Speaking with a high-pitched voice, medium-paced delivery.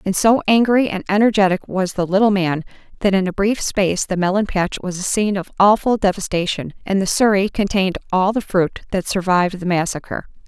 Yes: high, 195 Hz; average, 195 wpm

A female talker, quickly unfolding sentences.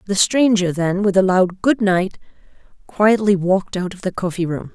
No: female; average, 190 wpm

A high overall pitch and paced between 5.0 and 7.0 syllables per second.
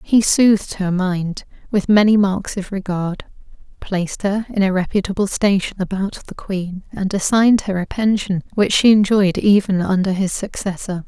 No: high, 195 Hz; 4.7 syllables/s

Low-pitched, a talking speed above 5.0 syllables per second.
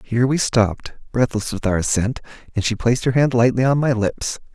Yes: low, 120 Hz; 5.7 syllables/s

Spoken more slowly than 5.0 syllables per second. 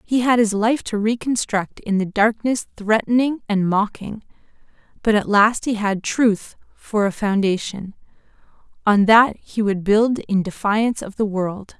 Yes: 4.2 syllables/s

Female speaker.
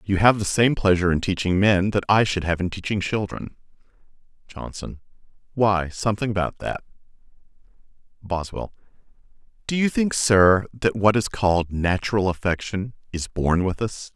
No: male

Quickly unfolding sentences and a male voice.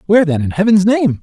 Yes: fast, 245 wpm; male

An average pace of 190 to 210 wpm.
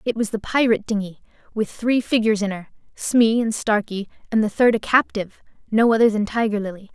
Yes: average, 200 wpm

